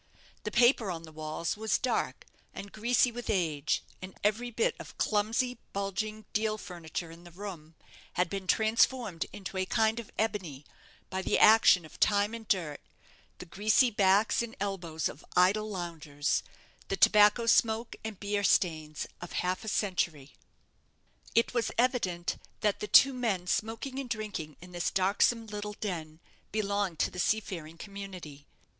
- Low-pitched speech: No, high, 200 Hz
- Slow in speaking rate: No, average, 155 wpm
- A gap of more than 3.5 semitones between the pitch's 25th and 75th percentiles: Yes, average, 4.0 semitones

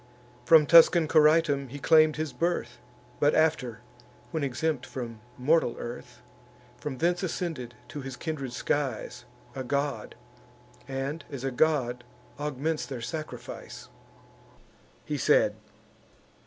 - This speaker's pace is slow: Yes, slow, 115 wpm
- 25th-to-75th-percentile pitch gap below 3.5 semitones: No, average, 3.8 semitones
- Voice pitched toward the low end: No, medium, 145 Hz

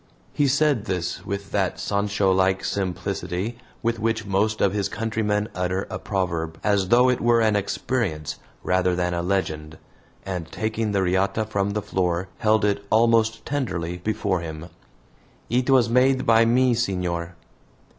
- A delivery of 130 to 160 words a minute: Yes, average, 155 wpm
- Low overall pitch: Yes, low, 100 Hz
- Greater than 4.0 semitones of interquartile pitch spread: No, average, 3.7 semitones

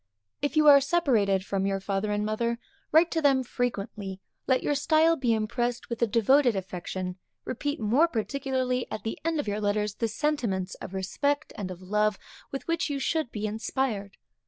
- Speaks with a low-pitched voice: No, high, 235 Hz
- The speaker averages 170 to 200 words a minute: Yes, average, 180 wpm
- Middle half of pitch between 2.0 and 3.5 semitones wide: No, wide, 5.6 semitones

